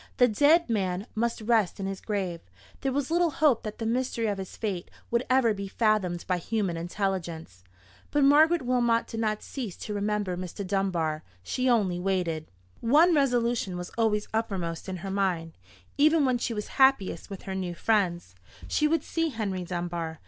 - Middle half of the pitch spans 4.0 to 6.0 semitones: Yes, average, 5.1 semitones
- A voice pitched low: No, high, 210 Hz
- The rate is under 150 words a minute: No, average, 180 wpm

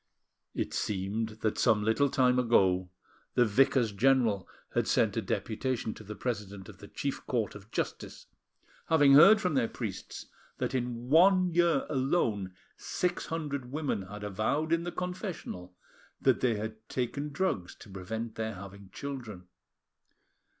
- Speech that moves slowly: No, average, 150 wpm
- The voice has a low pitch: Yes, low, 120 Hz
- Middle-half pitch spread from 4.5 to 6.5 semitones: Yes, wide, 5.5 semitones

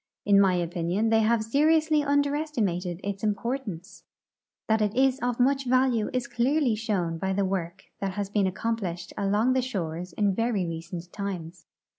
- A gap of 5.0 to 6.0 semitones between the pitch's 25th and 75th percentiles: Yes, average, 5.3 semitones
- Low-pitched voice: No, high, 205 Hz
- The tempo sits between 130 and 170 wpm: Yes, average, 165 wpm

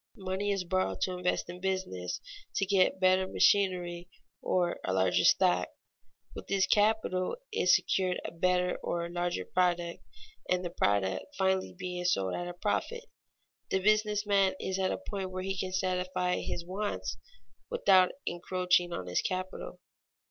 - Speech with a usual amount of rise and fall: No, narrow, 1.4 semitones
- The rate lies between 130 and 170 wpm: Yes, average, 155 wpm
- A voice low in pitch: No, medium, 185 Hz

